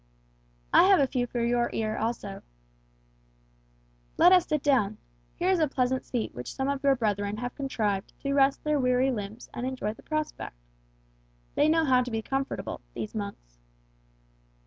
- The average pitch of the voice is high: Yes, very high, 250 Hz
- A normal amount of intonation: Yes, average, 4.4 semitones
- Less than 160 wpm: No, average, 165 wpm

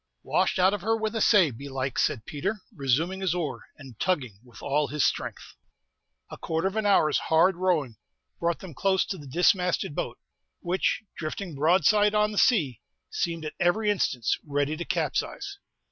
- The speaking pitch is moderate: Yes, medium, 170 Hz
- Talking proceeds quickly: No, average, 175 wpm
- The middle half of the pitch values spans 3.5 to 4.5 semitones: No, average, 5.2 semitones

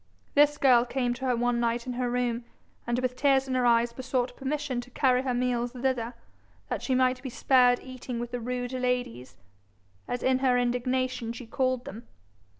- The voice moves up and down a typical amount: No, narrow, 1.1 semitones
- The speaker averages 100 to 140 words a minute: No, average, 190 wpm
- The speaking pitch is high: Yes, very high, 250 Hz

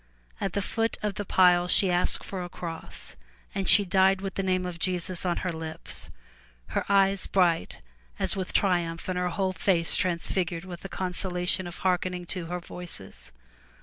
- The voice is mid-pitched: Yes, medium, 180 Hz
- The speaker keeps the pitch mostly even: Yes, narrow, 1.5 semitones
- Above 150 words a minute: Yes, average, 180 wpm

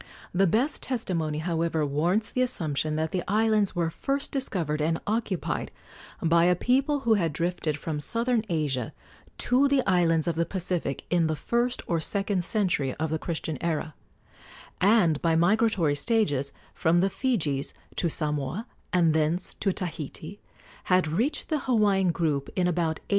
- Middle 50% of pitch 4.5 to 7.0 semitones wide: Yes, average, 5.2 semitones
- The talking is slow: No, average, 160 wpm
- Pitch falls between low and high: Yes, medium, 175 Hz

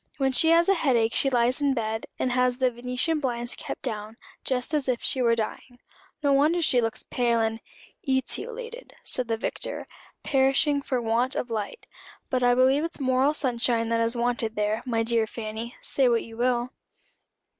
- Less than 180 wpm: No, average, 190 wpm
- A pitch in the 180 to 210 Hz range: No, high, 245 Hz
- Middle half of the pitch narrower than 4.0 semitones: Yes, average, 2.7 semitones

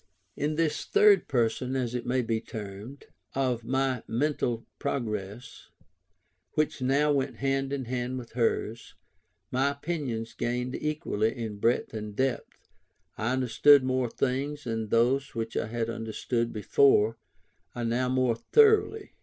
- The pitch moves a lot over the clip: No, average, 3.1 semitones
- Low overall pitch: Yes, low, 125 Hz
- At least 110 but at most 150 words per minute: Yes, average, 140 wpm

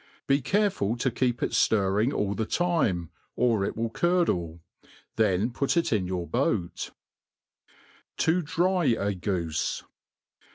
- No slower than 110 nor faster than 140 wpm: Yes, slow, 135 wpm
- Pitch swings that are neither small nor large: No, wide, 8.8 semitones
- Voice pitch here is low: Yes, low, 115 Hz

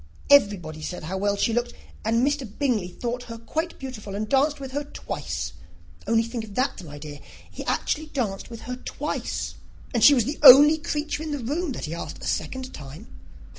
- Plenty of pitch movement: Yes, wide, 5.8 semitones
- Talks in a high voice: Yes, high, 240 Hz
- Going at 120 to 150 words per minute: No, average, 200 wpm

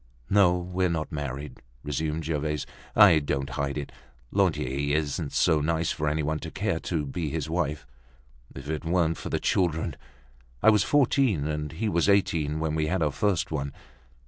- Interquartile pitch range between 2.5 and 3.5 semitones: Yes, average, 3.2 semitones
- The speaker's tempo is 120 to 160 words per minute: No, average, 175 wpm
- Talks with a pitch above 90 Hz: No, very low, 80 Hz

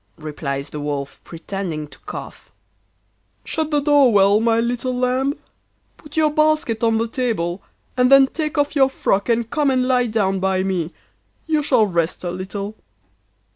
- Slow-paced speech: No, average, 165 wpm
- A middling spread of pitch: No, wide, 6.4 semitones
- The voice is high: Yes, high, 230 Hz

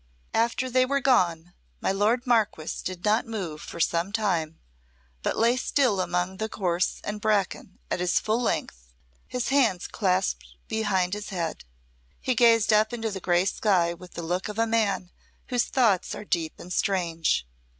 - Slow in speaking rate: No, average, 170 wpm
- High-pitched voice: Yes, high, 195 Hz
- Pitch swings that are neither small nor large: Yes, average, 4.4 semitones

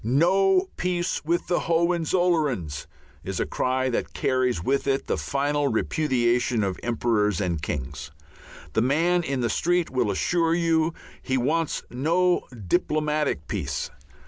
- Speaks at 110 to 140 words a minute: Yes, slow, 135 wpm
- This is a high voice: No, medium, 140 Hz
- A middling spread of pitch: No, wide, 6.1 semitones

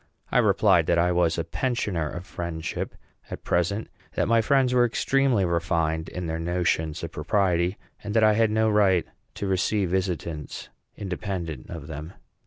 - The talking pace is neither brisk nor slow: Yes, average, 160 wpm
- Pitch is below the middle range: Yes, very low, 90 Hz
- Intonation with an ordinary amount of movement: Yes, average, 4.0 semitones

